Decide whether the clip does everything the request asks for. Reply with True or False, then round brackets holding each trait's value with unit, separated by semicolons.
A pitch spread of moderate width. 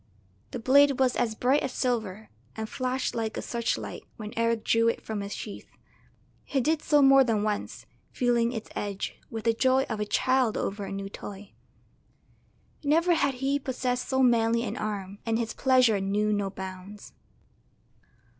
True (3.7 semitones)